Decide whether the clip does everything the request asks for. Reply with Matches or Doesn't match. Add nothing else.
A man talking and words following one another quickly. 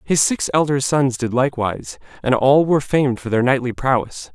Doesn't match